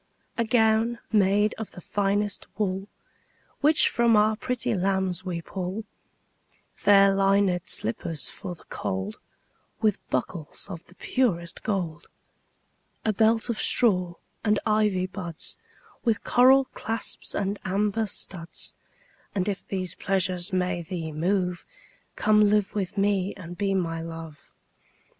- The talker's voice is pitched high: Yes, high, 195 Hz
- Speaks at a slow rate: Yes, slow, 130 wpm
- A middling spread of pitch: Yes, average, 3.1 semitones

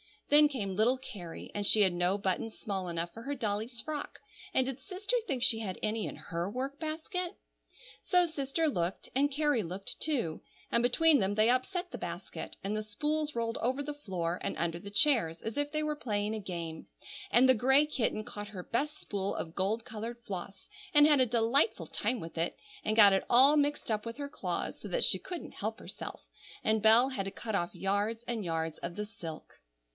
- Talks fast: Yes, fast, 210 wpm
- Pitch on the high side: Yes, high, 225 Hz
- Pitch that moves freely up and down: Yes, wide, 6.3 semitones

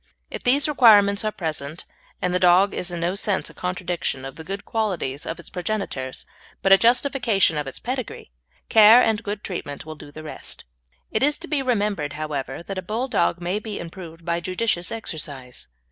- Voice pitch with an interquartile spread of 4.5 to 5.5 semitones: Yes, average, 5.1 semitones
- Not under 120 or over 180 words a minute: No, average, 190 wpm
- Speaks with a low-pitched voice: No, medium, 185 Hz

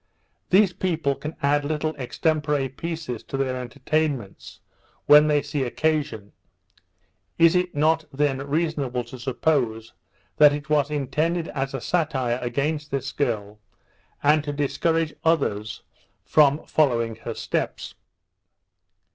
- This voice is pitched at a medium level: Yes, medium, 145 Hz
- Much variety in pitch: No, average, 3.3 semitones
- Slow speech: Yes, slow, 120 wpm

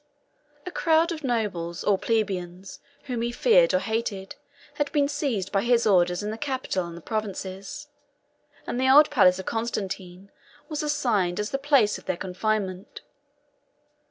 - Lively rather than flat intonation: Yes, wide, 6.7 semitones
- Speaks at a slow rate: No, average, 155 wpm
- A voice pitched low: No, high, 220 Hz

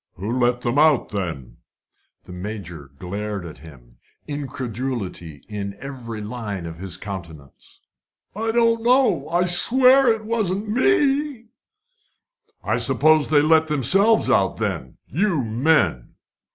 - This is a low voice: Yes, low, 130 Hz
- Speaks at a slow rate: Yes, slow, 125 wpm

